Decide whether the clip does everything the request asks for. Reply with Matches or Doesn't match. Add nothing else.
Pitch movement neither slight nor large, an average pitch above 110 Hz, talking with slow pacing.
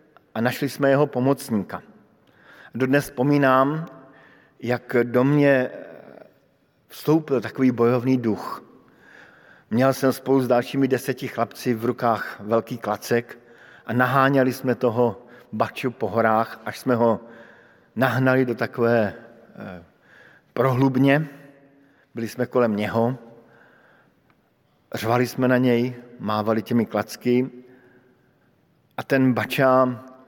Doesn't match